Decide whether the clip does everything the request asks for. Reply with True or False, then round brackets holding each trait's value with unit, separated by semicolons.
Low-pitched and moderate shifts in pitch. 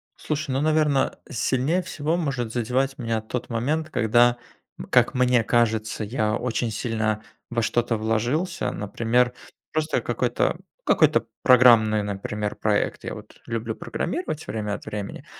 True (120 Hz; 3.7 semitones)